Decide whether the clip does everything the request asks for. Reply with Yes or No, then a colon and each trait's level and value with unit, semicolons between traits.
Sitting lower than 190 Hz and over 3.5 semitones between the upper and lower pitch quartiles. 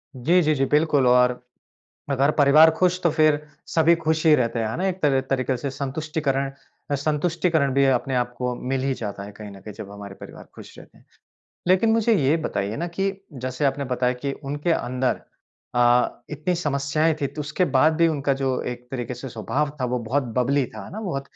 Yes: medium, 140 Hz; average, 3.9 semitones